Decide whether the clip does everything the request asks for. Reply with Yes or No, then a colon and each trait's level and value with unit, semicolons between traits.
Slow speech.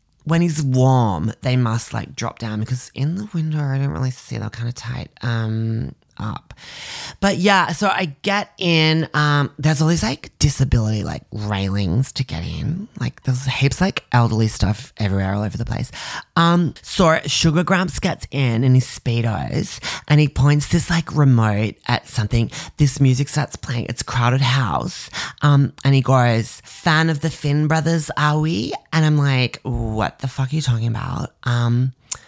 No: average, 180 wpm